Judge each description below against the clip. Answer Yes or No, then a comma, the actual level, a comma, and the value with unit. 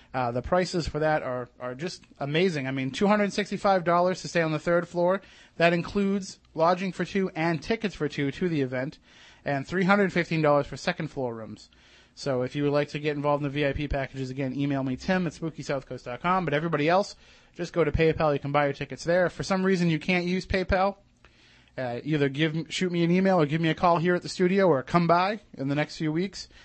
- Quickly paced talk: Yes, fast, 220 wpm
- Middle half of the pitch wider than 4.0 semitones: Yes, average, 4.4 semitones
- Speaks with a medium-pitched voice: Yes, medium, 160 Hz